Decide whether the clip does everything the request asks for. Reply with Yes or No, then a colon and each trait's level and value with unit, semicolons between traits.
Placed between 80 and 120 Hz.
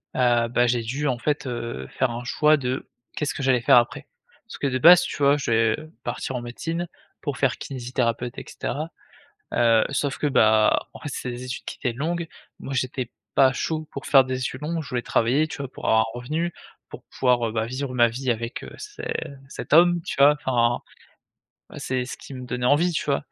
No: low, 130 Hz